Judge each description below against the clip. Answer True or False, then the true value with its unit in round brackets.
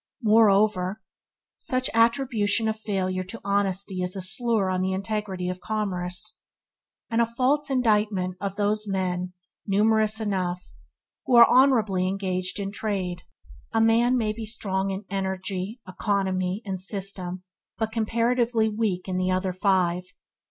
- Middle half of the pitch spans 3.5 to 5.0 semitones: False (3.1 semitones)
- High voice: True (200 Hz)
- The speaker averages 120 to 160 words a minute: True (140 wpm)